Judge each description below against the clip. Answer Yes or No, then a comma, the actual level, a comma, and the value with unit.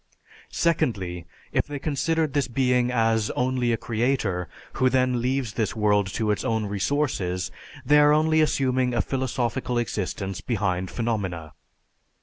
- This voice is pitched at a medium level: No, low, 120 Hz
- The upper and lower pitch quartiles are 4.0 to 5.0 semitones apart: Yes, average, 4.4 semitones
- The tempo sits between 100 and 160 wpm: Yes, slow, 135 wpm